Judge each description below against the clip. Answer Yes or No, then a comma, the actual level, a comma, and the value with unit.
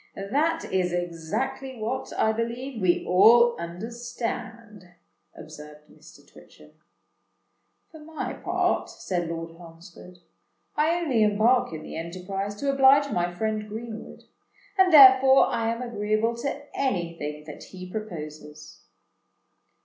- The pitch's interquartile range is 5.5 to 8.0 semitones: Yes, wide, 6.4 semitones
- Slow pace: Yes, slow, 120 wpm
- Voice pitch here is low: No, high, 215 Hz